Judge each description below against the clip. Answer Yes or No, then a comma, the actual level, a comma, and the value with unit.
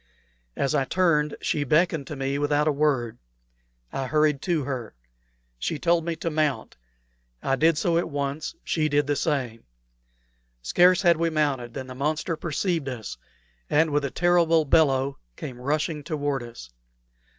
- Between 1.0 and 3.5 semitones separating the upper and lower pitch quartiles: Yes, average, 3.1 semitones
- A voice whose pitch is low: No, medium, 150 Hz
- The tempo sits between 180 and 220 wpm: No, average, 160 wpm